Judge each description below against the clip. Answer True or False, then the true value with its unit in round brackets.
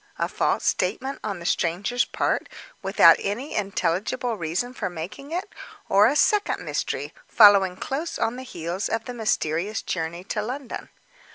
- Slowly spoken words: False (155 wpm)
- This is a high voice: True (210 Hz)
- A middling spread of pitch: False (5.9 semitones)